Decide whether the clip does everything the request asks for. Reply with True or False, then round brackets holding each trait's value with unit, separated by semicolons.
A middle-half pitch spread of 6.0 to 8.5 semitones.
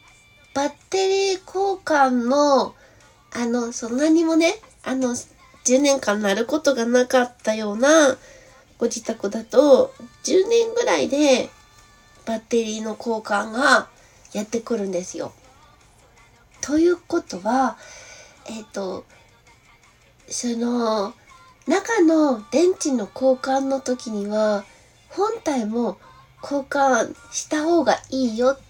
False (5.4 semitones)